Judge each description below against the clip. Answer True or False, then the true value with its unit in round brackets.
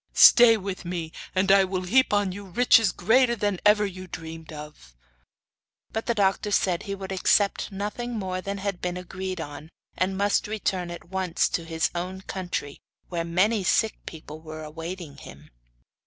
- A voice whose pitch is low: False (190 Hz)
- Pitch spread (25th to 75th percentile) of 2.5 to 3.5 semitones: True (3.0 semitones)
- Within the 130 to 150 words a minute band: False (170 wpm)